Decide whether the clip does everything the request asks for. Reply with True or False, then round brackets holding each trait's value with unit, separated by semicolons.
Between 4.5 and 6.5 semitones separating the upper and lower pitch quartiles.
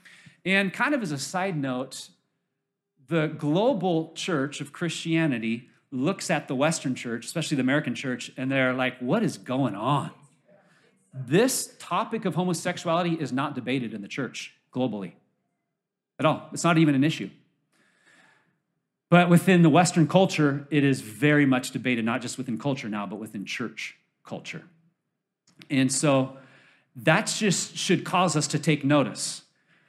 True (4.8 semitones)